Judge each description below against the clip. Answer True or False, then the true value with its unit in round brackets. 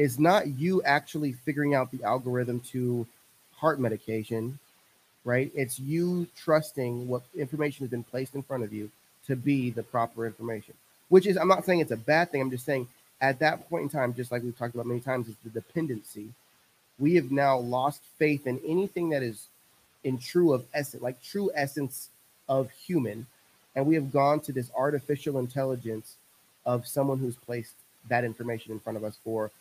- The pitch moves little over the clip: False (3.5 semitones)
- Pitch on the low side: True (130 Hz)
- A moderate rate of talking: True (190 wpm)